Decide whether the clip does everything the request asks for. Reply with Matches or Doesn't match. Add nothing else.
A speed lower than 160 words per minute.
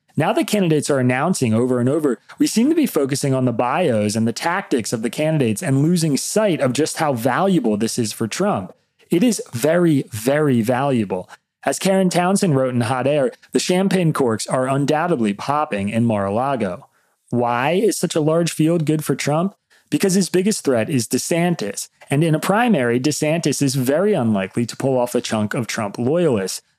Doesn't match